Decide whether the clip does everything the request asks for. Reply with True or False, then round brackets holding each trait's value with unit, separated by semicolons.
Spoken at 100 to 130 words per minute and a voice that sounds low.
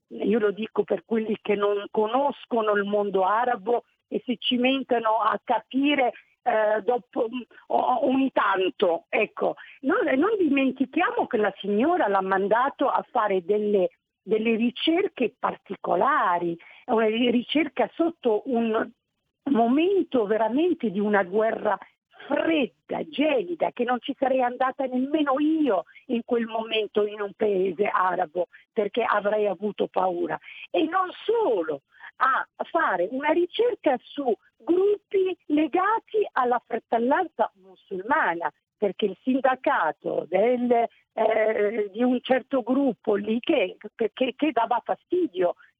False (125 wpm; 240 Hz)